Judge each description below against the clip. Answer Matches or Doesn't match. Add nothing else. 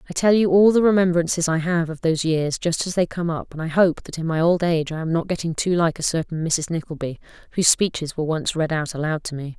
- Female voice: Matches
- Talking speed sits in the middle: Doesn't match